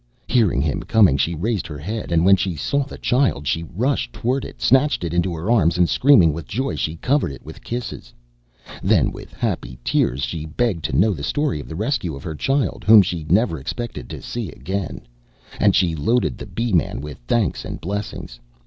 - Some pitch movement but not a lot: No, wide, 7.0 semitones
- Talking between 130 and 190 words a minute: No, fast, 205 wpm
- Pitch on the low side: Yes, very low, 90 Hz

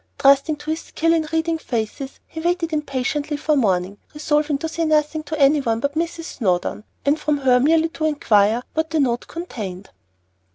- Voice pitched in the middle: No, very high, 295 Hz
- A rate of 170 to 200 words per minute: Yes, average, 175 wpm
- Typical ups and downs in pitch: Yes, average, 4.3 semitones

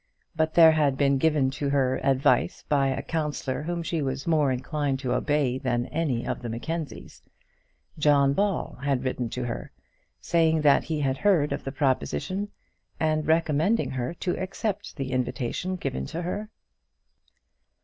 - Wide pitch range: No, average, 3.6 semitones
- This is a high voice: No, medium, 145 Hz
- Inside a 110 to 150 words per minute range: No, average, 160 wpm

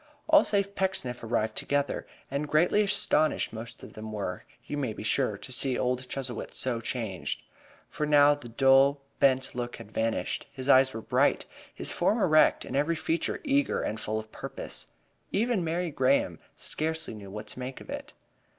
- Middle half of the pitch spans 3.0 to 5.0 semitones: No, wide, 5.4 semitones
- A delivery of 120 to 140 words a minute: No, average, 180 wpm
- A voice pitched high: No, low, 135 Hz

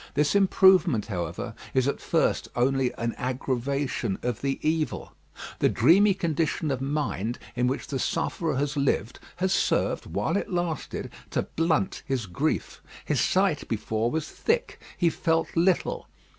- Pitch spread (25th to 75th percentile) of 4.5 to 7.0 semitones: Yes, average, 5.1 semitones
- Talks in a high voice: No, medium, 145 Hz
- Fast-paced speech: No, average, 145 wpm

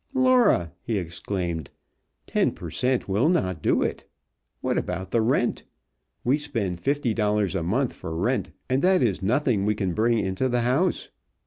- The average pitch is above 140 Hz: No, low, 110 Hz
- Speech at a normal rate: Yes, average, 160 wpm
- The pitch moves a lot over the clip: Yes, wide, 5.7 semitones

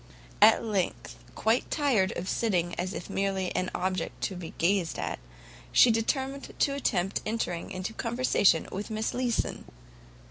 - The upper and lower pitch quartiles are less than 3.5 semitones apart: No, average, 3.9 semitones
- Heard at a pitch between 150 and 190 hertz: No, high, 200 Hz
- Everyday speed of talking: Yes, average, 145 wpm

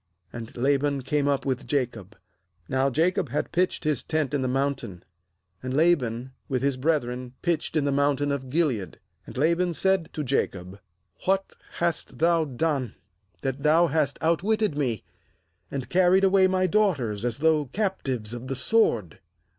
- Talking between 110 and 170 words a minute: Yes, average, 155 wpm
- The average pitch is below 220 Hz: Yes, medium, 140 Hz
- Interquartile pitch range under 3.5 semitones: No, average, 4.8 semitones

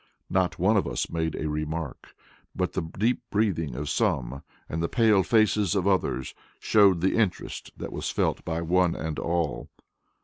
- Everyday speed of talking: Yes, average, 170 wpm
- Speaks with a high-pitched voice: No, very low, 85 Hz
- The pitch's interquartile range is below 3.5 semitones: No, average, 3.8 semitones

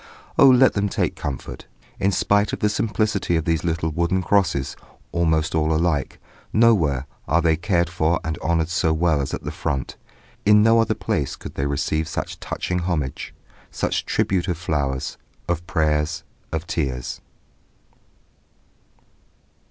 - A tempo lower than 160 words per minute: Yes, average, 150 wpm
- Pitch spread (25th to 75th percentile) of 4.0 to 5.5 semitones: No, average, 3.4 semitones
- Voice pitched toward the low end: Yes, very low, 85 Hz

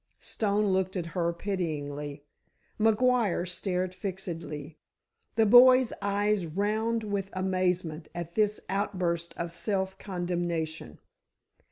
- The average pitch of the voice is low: No, medium, 185 Hz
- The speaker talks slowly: Yes, slow, 100 wpm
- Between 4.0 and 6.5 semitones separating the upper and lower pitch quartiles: No, average, 3.3 semitones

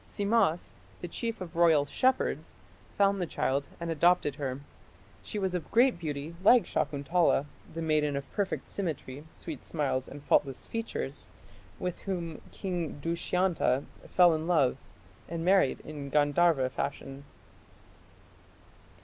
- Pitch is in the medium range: Yes, medium, 165 Hz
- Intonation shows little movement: No, average, 4.1 semitones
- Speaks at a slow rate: Yes, slow, 130 wpm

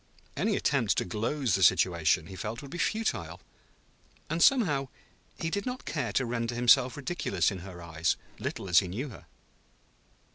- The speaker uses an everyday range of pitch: No, wide, 8.2 semitones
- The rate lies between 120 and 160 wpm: No, average, 170 wpm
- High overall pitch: No, low, 120 Hz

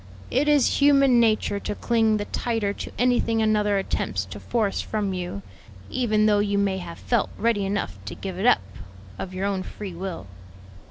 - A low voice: No, high, 205 Hz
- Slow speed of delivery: No, average, 180 wpm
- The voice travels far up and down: No, average, 3.2 semitones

